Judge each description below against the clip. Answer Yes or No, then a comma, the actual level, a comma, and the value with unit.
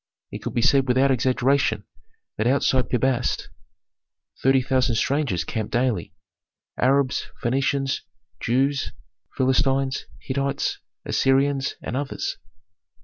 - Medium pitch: No, low, 130 Hz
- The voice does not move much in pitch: Yes, narrow, 1.5 semitones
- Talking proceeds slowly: Yes, slow, 105 wpm